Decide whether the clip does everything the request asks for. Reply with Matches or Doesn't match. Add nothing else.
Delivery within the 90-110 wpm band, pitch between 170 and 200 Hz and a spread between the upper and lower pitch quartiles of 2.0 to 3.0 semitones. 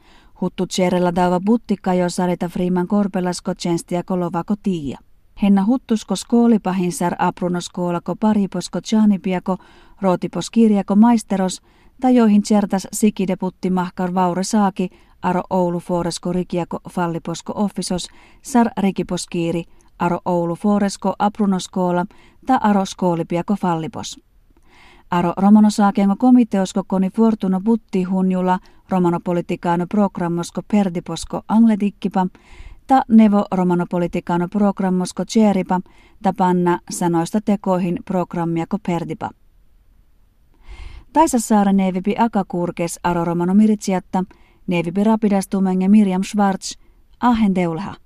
Matches